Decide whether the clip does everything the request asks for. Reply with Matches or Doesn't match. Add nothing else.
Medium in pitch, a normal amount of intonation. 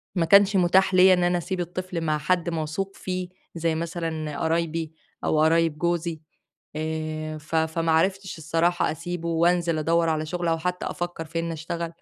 Doesn't match